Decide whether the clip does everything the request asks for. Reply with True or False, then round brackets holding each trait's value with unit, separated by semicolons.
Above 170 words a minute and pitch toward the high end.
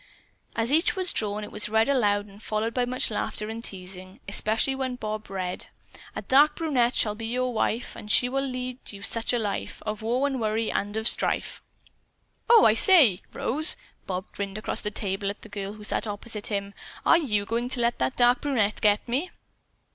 True (205 wpm; 220 Hz)